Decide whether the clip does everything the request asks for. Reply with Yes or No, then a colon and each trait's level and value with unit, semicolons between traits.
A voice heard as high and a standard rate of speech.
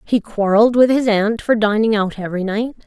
No: high, 220 Hz; fast, 210 wpm